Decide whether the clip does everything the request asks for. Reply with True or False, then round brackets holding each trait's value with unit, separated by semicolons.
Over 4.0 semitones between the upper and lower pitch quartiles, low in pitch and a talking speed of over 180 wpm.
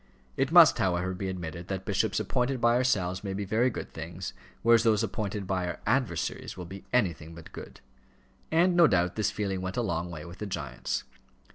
True (4.6 semitones; 95 Hz; 200 wpm)